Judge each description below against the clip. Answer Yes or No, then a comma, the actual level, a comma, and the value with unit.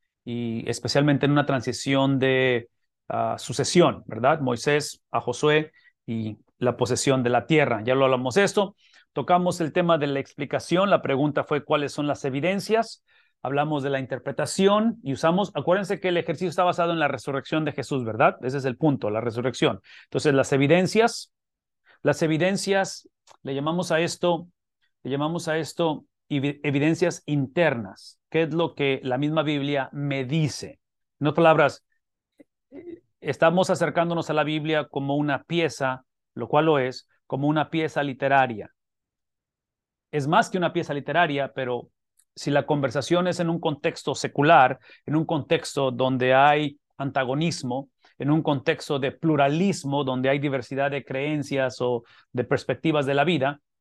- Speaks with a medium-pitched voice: Yes, medium, 145 Hz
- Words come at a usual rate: Yes, average, 155 wpm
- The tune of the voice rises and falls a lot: No, average, 3.6 semitones